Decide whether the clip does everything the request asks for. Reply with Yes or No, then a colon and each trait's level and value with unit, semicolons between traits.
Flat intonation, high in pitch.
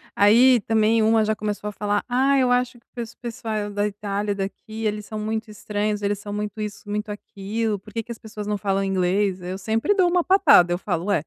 Yes: narrow, 1.8 semitones; high, 210 Hz